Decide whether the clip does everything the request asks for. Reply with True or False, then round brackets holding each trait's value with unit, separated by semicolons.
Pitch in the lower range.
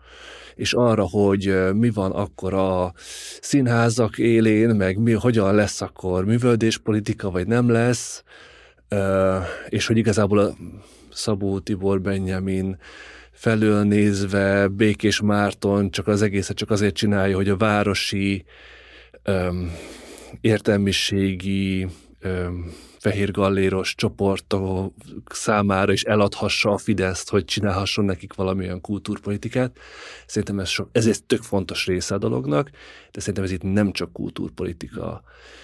True (100 Hz)